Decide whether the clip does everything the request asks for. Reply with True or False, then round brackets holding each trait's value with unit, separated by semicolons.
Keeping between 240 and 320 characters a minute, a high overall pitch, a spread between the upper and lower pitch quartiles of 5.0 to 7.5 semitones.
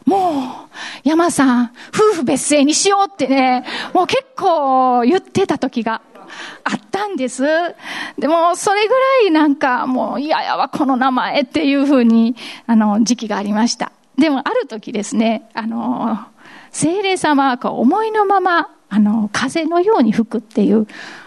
True (295 characters per minute; 280 Hz; 6.3 semitones)